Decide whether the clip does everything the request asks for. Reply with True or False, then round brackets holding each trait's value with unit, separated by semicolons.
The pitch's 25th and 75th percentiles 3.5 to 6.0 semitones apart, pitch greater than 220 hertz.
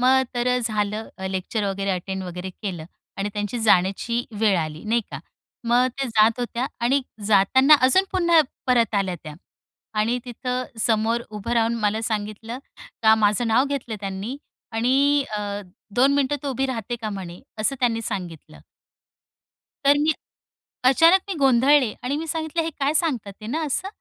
True (4.4 semitones; 230 Hz)